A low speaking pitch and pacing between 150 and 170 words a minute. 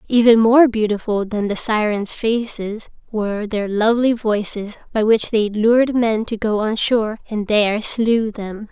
No: high, 220 Hz; average, 165 wpm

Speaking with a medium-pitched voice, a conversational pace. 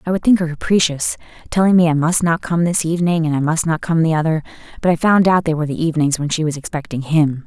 No: medium, 160 Hz; fast, 255 wpm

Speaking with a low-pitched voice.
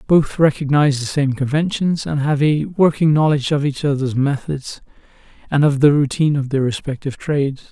No: medium, 145 Hz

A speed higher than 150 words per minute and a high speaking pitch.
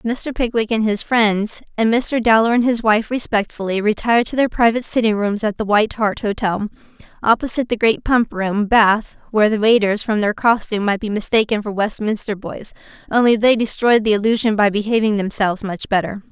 Yes: average, 190 wpm; high, 215 Hz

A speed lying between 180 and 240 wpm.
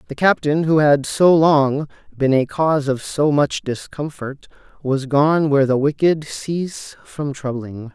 No: average, 160 wpm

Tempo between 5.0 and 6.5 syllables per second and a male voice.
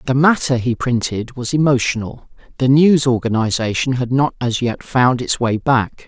No: 4.7 syllables/s; male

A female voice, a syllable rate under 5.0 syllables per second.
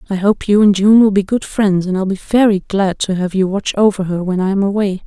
No: female; 5.4 syllables/s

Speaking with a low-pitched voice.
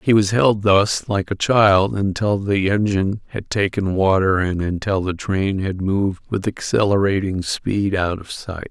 Yes: low, 100 Hz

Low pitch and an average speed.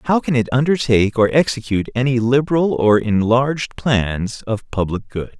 Yes: low, 125 Hz; average, 155 wpm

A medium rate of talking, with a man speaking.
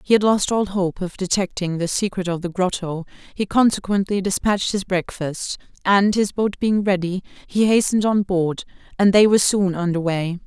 No: average, 185 wpm; female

